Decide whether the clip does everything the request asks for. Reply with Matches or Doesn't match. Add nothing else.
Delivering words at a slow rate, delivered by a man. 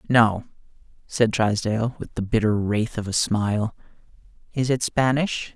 Matches